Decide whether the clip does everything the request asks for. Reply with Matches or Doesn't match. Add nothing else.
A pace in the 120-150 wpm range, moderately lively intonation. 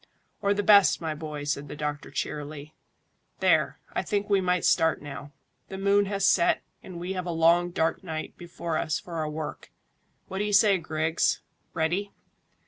Doesn't match